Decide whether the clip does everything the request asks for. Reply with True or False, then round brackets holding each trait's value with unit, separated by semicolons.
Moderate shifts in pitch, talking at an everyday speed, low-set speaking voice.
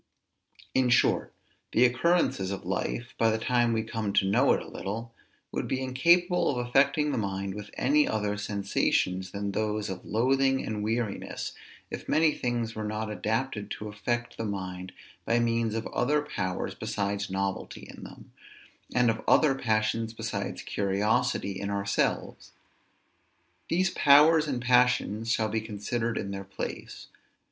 True (3.7 semitones; 155 wpm; 110 Hz)